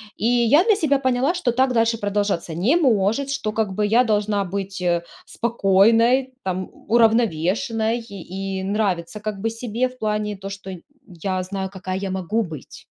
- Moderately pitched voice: No, high, 210 Hz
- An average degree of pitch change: Yes, average, 3.6 semitones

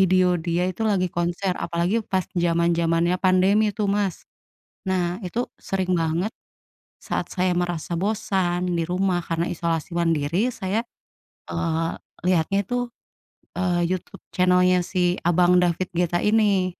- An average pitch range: No, narrow, 1.7 semitones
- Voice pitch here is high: No, medium, 180 Hz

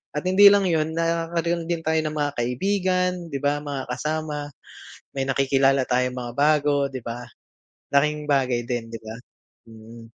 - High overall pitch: No, medium, 145 Hz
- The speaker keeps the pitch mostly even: No, average, 4.3 semitones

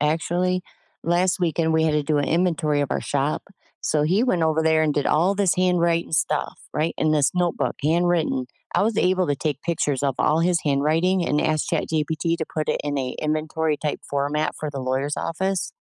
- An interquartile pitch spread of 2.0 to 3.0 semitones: Yes, average, 2.7 semitones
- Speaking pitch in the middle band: Yes, medium, 160 Hz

